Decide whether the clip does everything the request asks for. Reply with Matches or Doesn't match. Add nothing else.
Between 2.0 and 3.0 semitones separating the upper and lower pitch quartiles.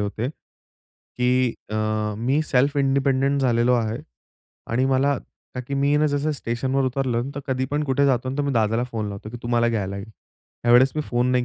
Matches